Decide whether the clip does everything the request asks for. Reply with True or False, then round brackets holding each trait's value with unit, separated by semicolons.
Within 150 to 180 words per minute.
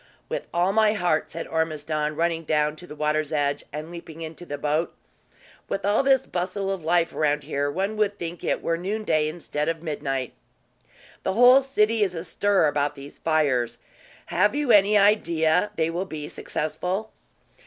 True (170 wpm)